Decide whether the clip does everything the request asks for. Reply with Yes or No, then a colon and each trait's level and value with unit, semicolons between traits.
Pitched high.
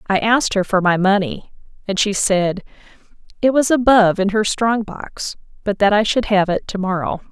Yes: high, 205 Hz